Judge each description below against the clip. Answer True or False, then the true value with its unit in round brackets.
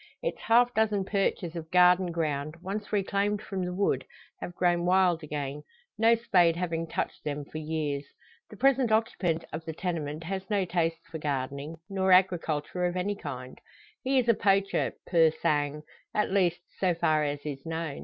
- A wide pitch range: False (4.2 semitones)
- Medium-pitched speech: True (175 Hz)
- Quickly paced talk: False (175 wpm)